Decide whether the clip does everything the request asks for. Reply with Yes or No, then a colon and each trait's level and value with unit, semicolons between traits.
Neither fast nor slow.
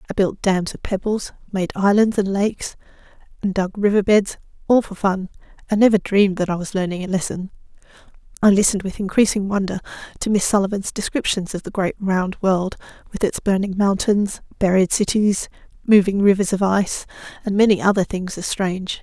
Yes: average, 175 wpm